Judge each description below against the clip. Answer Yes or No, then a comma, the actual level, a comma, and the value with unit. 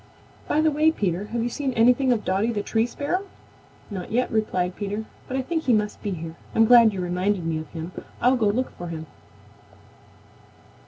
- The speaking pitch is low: No, high, 220 Hz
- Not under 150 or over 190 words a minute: No, average, 200 wpm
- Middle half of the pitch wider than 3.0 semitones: Yes, average, 5.3 semitones